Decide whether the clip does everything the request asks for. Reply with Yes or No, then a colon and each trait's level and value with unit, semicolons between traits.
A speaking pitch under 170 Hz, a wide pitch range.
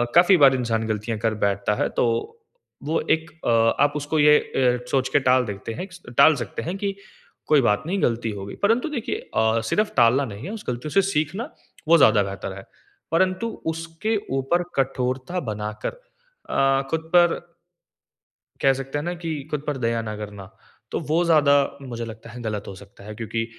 Yes: low, 135 Hz; wide, 6.6 semitones